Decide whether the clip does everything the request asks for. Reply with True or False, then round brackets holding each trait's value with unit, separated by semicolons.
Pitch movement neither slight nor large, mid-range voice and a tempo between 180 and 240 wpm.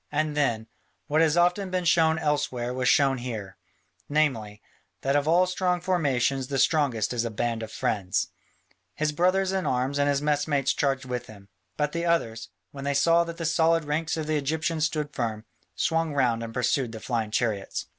True (4.8 semitones; 145 Hz; 190 wpm)